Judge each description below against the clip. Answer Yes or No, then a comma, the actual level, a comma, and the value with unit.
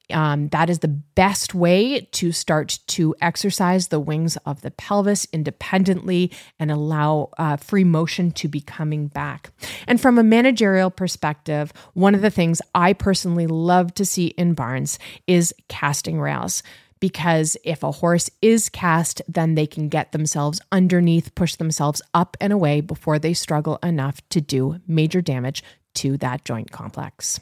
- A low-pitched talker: No, medium, 165 Hz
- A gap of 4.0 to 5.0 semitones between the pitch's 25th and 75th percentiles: No, average, 3.2 semitones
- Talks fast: No, average, 160 wpm